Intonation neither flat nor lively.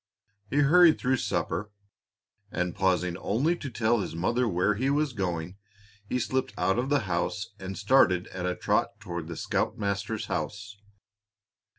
No: wide, 5.8 semitones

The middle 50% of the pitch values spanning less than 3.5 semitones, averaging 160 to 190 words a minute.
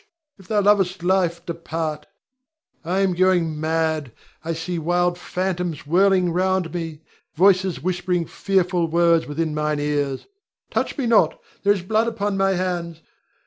No: narrow, 2.5 semitones; average, 140 wpm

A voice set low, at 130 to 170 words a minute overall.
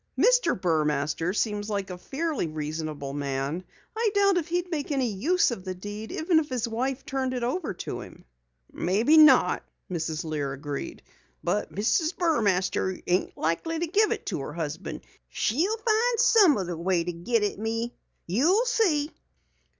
No: high, 220 Hz; average, 160 wpm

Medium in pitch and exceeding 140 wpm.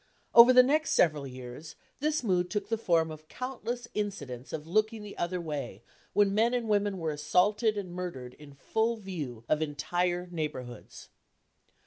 Yes: medium, 180 Hz; average, 160 wpm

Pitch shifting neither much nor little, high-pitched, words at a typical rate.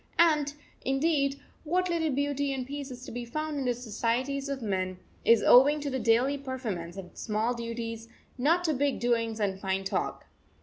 Yes: average, 3.8 semitones; very high, 255 Hz; average, 185 wpm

